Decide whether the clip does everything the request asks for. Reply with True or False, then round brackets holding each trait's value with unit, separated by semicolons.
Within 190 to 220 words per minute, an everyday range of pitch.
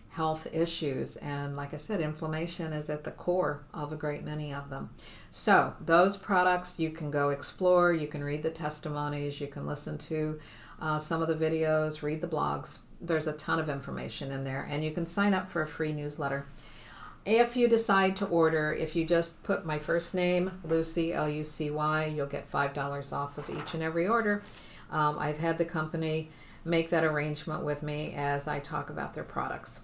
False (200 wpm; 2.2 semitones)